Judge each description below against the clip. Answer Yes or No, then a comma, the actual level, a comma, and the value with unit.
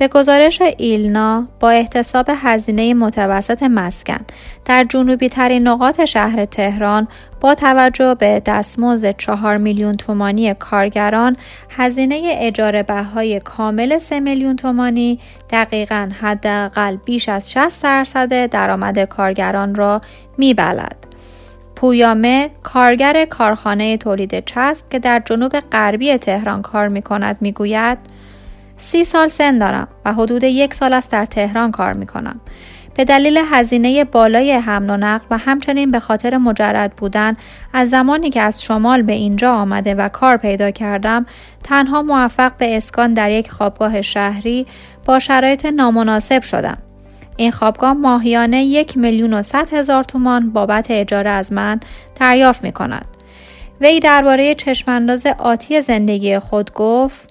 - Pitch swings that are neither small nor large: Yes, average, 3.9 semitones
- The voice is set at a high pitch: Yes, high, 235 Hz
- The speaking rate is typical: Yes, average, 130 wpm